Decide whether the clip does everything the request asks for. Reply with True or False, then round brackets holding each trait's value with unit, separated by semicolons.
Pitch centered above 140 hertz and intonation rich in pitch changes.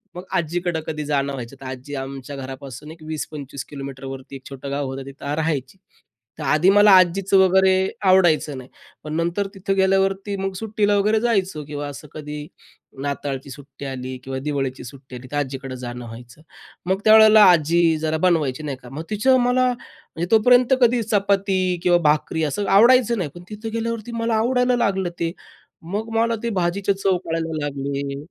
True (160 Hz; 6.3 semitones)